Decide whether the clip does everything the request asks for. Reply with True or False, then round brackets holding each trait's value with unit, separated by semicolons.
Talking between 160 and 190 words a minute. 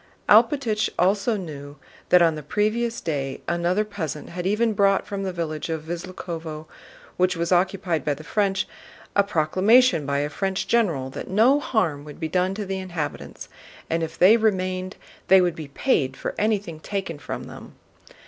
True (170 wpm)